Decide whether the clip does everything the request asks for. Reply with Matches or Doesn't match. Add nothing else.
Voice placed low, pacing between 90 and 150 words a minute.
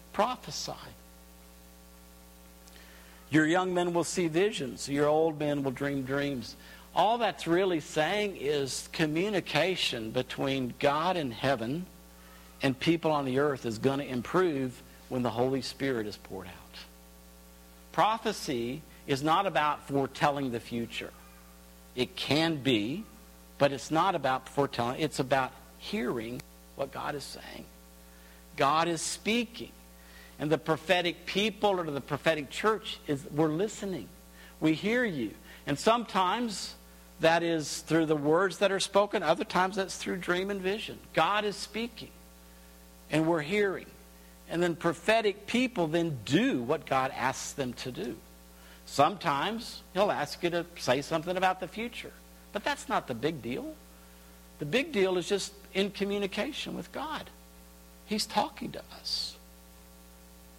Doesn't match